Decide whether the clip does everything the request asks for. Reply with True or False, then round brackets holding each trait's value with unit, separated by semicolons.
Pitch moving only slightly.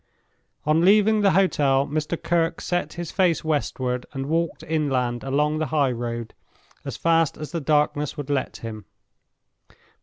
False (3.6 semitones)